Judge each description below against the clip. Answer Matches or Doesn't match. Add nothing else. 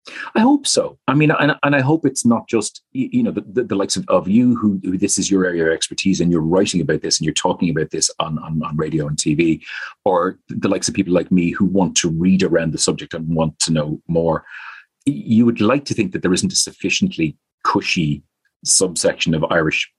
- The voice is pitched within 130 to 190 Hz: Doesn't match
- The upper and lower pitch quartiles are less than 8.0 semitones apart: Doesn't match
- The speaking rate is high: Matches